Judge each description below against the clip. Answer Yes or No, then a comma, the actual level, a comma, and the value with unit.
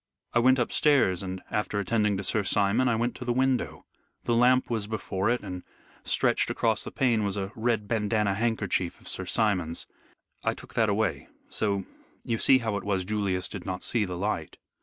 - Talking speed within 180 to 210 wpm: Yes, average, 195 wpm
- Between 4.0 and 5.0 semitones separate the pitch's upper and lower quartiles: No, average, 3.3 semitones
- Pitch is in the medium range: No, low, 105 Hz